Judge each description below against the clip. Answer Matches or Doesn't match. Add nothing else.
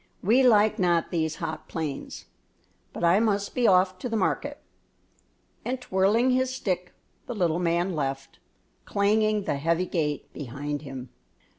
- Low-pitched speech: Doesn't match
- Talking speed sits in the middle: Matches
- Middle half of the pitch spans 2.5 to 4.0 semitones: Doesn't match